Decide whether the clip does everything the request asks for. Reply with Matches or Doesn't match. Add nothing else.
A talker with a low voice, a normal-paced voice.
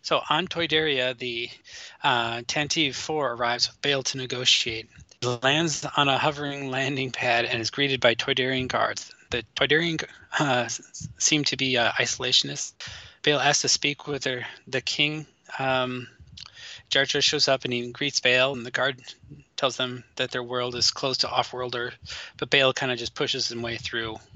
Matches